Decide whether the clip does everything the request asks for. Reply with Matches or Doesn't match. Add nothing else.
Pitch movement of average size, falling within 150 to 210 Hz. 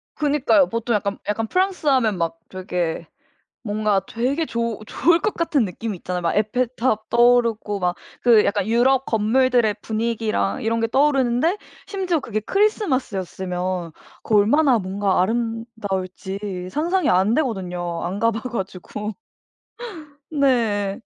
Doesn't match